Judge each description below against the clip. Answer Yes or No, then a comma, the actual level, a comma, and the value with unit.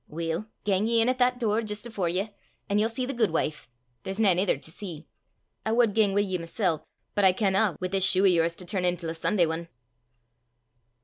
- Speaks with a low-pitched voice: No, high, 195 Hz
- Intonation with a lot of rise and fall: No, average, 4.1 semitones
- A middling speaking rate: No, fast, 215 wpm